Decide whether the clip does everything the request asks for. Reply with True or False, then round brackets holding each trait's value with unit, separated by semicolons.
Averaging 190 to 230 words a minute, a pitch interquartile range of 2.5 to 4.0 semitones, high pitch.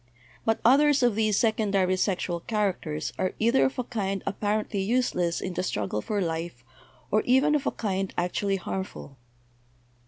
False (155 wpm; 3.7 semitones; 200 Hz)